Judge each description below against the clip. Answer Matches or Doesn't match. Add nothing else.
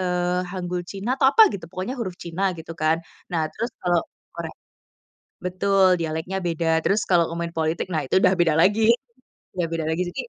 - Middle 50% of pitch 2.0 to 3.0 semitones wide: Matches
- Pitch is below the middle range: Doesn't match